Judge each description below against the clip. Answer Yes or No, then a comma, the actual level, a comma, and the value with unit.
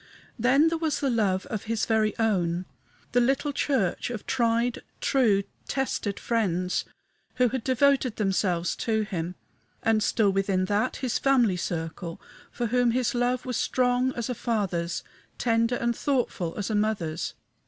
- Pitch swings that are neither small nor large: Yes, average, 4.3 semitones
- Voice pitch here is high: Yes, high, 225 Hz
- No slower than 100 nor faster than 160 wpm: Yes, average, 155 wpm